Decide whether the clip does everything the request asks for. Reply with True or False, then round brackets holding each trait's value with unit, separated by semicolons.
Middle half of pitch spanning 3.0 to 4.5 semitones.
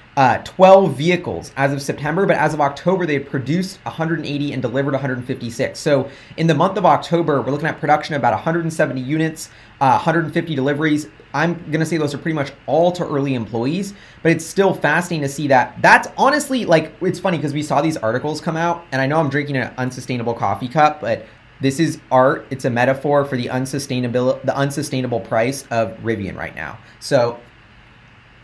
True (3.9 semitones)